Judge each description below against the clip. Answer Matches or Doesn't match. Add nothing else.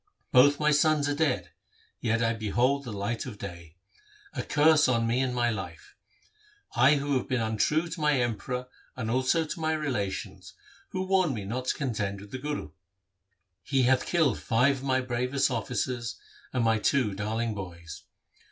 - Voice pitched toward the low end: Matches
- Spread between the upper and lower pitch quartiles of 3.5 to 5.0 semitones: Matches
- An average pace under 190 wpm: Matches